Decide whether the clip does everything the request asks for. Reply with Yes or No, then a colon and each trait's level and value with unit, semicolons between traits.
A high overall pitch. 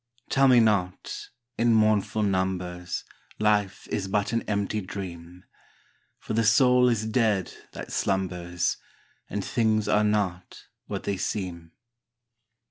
No: low, 100 Hz